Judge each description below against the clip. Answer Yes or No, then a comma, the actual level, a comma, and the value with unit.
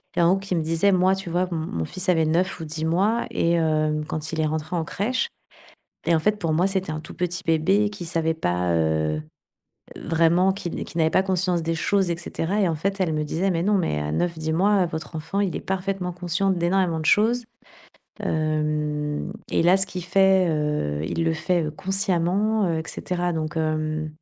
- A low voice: No, medium, 170 Hz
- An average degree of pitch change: Yes, average, 3.2 semitones